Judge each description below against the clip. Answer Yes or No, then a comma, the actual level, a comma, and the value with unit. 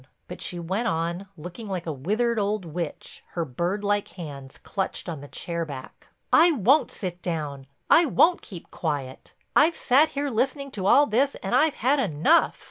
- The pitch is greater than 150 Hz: Yes, high, 190 Hz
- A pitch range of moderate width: No, wide, 7.7 semitones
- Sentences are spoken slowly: No, average, 185 wpm